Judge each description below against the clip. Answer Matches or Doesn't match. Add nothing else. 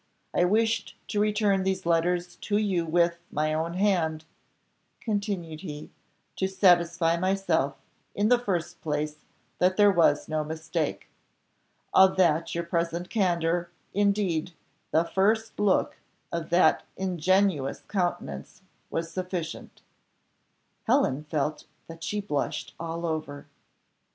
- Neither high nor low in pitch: Matches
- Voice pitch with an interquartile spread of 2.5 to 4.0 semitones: Matches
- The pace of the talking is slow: Matches